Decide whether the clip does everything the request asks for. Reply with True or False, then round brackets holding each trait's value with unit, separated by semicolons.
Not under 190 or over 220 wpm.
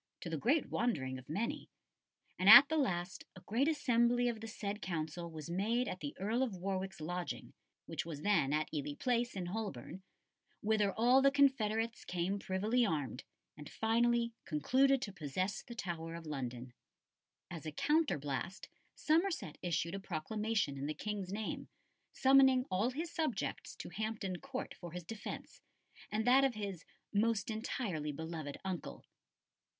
False (155 wpm)